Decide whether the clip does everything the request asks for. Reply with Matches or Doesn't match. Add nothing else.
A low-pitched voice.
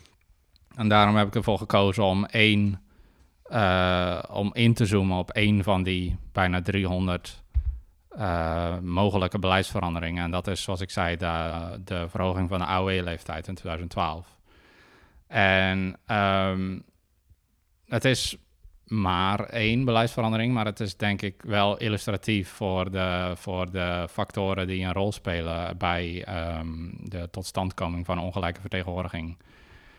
Matches